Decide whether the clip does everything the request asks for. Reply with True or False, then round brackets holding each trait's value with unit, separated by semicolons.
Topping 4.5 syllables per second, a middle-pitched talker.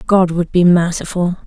True (4.7 syllables/s; 175 Hz)